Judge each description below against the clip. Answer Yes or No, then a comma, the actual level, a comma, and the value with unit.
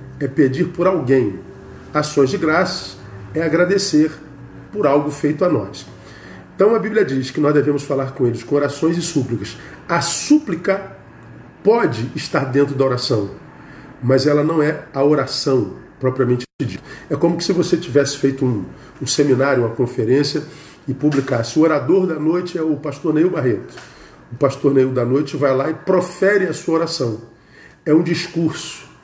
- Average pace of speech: Yes, average, 165 wpm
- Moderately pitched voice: Yes, medium, 145 Hz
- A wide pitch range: No, average, 3.5 semitones